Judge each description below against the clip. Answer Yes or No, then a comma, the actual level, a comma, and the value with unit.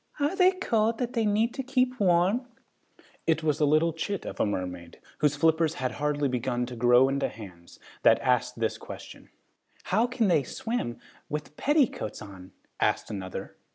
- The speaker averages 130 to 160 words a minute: No, average, 170 wpm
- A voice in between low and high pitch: Yes, medium, 155 Hz